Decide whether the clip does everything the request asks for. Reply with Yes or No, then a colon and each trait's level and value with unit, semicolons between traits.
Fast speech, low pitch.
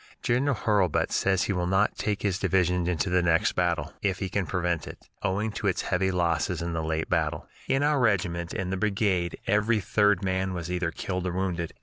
Yes: fast, 210 wpm; very low, 95 Hz